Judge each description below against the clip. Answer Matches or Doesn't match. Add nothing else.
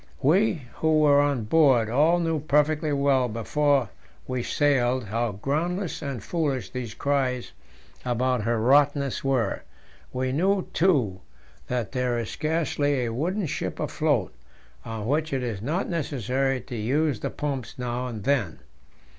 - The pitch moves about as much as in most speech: Matches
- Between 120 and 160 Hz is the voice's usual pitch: Matches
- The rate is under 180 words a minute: Matches